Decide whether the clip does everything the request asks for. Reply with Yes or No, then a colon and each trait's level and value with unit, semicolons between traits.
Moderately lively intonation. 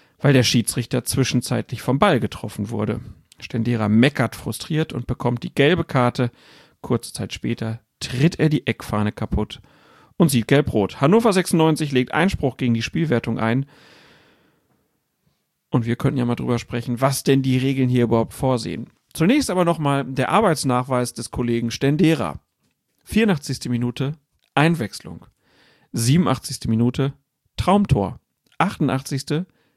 Yes: average, 4.0 semitones